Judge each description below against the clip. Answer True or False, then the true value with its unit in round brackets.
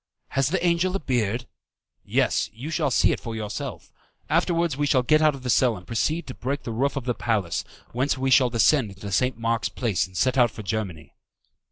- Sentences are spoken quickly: True (215 wpm)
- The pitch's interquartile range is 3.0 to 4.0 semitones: False (4.4 semitones)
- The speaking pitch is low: True (125 Hz)